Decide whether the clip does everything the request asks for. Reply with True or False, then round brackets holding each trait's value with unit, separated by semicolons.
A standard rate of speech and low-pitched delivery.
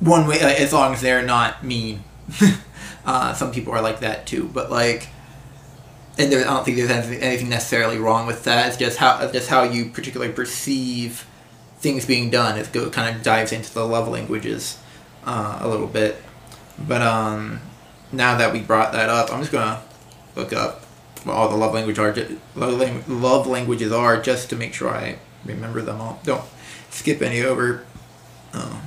True (180 wpm; 120 Hz)